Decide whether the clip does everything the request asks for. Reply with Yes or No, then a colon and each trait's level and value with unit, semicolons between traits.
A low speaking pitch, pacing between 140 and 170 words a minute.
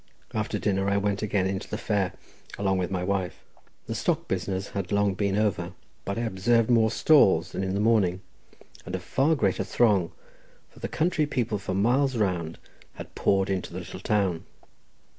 No: low, 100 Hz; average, 180 wpm